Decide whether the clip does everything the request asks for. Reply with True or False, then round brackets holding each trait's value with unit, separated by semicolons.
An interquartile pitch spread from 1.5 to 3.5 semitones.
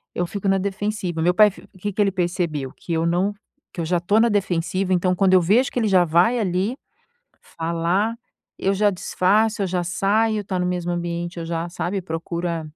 True (2.8 semitones)